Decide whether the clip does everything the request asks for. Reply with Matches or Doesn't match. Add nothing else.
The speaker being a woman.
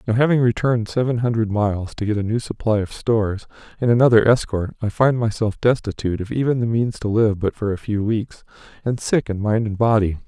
Doesn't match